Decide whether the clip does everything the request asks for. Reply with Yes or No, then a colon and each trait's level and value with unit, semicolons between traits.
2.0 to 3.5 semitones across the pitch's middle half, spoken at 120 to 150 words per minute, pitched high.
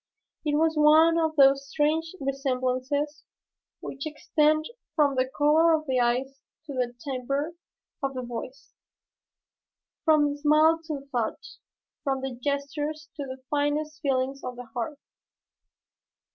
Yes: average, 2.7 semitones; slow, 135 wpm; very high, 285 Hz